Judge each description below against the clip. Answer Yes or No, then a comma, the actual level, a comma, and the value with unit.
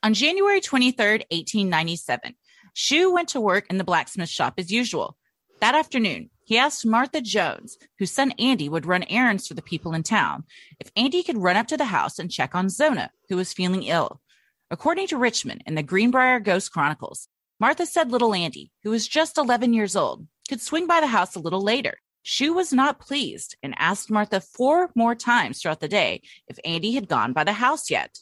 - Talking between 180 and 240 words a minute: Yes, average, 200 wpm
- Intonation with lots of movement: Yes, wide, 6.9 semitones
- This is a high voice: Yes, high, 230 Hz